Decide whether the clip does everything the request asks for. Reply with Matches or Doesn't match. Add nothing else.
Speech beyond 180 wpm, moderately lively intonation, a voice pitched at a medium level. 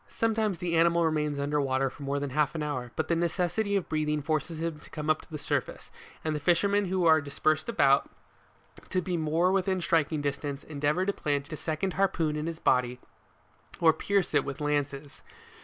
Matches